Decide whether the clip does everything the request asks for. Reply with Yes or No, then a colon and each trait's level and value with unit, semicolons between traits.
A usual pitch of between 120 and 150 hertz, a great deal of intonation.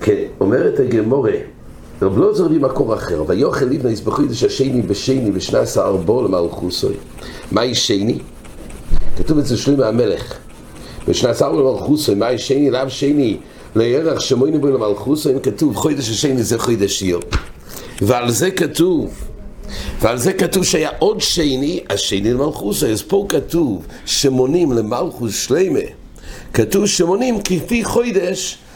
Yes: medium, 140 Hz; wide, 8.5 semitones